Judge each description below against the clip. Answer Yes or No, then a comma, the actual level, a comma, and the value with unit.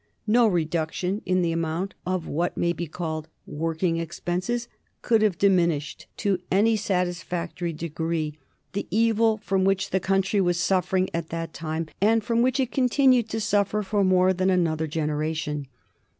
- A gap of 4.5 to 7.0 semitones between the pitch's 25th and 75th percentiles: No, average, 3.7 semitones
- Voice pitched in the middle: Yes, medium, 180 Hz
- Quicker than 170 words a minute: No, average, 155 wpm